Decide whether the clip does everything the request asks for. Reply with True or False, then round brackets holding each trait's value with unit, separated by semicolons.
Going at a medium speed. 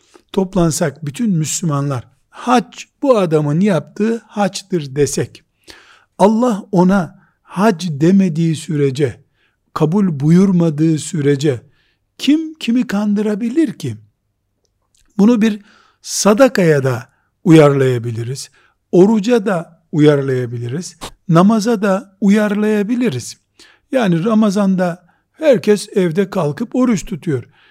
False (85 wpm)